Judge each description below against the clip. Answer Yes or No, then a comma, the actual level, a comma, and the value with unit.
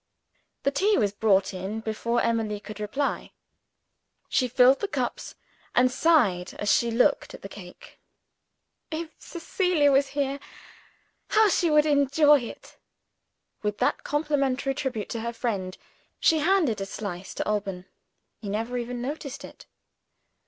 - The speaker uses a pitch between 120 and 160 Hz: No, very high, 250 Hz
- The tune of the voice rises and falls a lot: Yes, wide, 5.7 semitones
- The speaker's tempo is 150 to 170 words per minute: No, average, 140 wpm